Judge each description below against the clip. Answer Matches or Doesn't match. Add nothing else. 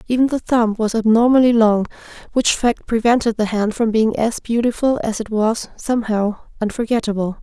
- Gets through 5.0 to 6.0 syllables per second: Matches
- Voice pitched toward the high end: Matches